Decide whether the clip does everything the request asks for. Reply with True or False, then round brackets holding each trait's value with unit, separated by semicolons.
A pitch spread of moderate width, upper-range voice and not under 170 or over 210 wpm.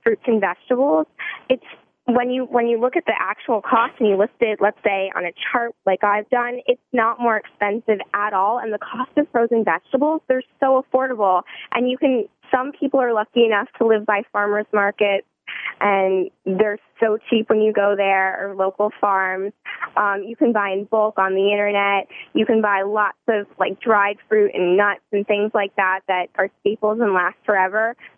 True (3.0 semitones; 210 Hz; 200 wpm)